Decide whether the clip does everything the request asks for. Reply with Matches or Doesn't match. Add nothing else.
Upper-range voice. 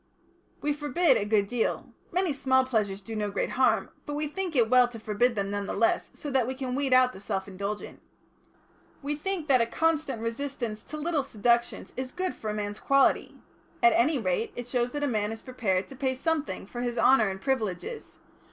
Matches